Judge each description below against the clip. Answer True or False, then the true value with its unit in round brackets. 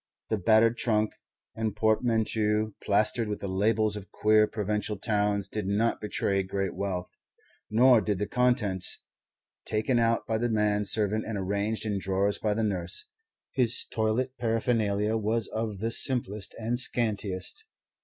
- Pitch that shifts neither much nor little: False (1.8 semitones)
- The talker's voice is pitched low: True (110 Hz)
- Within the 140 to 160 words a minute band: True (145 wpm)